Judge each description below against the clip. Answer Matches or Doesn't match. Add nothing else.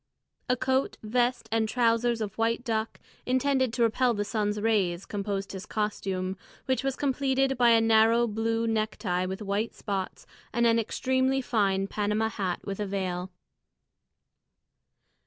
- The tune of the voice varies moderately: Matches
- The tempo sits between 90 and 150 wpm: Matches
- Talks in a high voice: Matches